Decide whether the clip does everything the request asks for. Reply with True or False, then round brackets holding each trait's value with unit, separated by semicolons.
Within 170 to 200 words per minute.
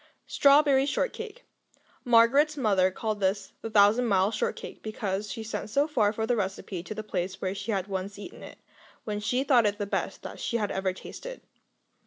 True (185 wpm)